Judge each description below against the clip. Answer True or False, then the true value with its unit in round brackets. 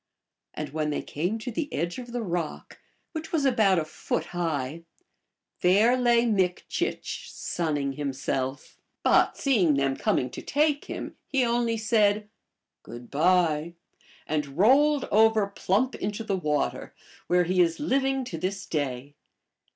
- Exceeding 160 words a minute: False (150 wpm)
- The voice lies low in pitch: False (185 Hz)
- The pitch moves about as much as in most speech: False (7.5 semitones)